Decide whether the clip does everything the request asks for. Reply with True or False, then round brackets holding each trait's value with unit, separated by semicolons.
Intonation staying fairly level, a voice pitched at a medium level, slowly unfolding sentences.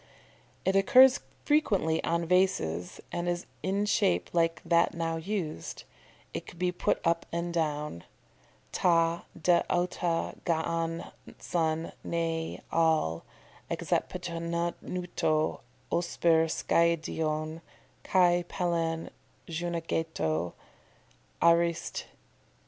True (1.3 semitones; 170 Hz; 95 wpm)